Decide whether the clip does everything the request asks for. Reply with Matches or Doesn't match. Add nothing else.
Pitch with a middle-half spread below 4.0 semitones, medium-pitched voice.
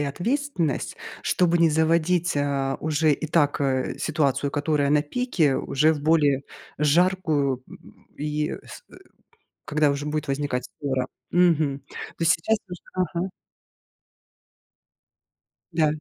Matches